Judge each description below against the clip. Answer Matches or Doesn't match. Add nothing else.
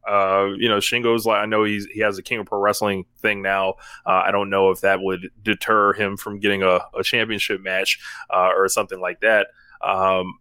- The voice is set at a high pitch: Doesn't match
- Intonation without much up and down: Matches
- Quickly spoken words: Matches